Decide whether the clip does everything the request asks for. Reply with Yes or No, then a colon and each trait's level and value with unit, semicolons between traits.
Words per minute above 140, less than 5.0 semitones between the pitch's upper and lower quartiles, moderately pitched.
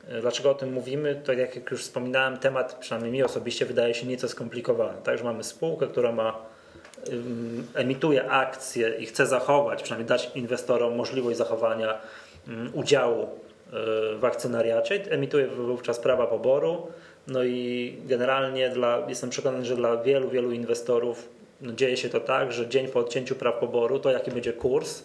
No: average, 155 wpm; average, 3.0 semitones; low, 125 Hz